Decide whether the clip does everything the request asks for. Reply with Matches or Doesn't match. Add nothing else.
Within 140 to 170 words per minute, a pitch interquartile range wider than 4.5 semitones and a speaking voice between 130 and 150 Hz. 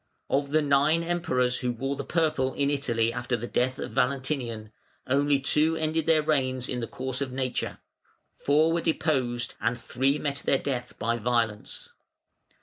Doesn't match